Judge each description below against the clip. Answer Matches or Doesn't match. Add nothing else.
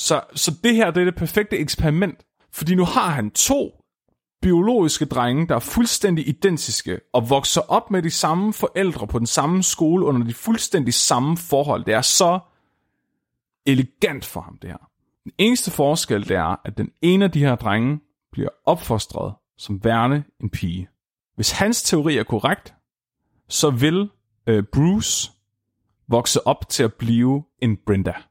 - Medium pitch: Matches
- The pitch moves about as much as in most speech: Doesn't match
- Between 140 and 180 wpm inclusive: Matches